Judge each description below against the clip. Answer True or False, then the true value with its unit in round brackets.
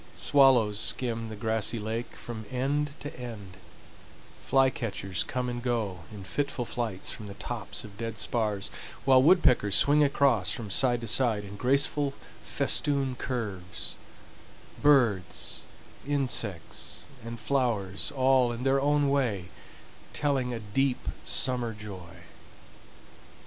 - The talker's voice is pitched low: True (120 Hz)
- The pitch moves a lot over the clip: False (4.3 semitones)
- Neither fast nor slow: False (125 wpm)